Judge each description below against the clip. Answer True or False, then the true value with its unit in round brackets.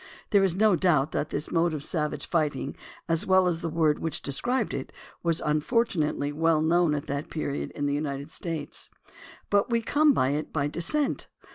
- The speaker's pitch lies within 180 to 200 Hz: False (160 Hz)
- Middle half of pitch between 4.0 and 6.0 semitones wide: False (3.6 semitones)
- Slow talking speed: False (185 wpm)